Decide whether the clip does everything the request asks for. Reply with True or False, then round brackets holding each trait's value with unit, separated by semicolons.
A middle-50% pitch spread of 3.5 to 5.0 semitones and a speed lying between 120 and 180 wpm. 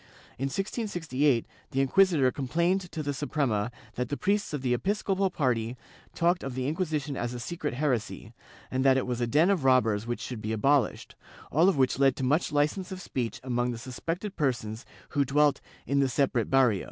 False (4.5 semitones; 190 wpm)